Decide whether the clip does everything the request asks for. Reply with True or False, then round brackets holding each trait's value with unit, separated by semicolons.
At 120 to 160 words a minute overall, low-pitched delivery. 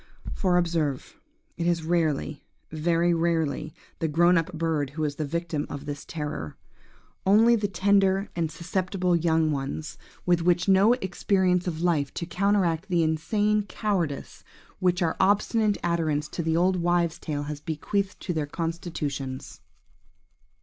False (135 wpm; 170 Hz)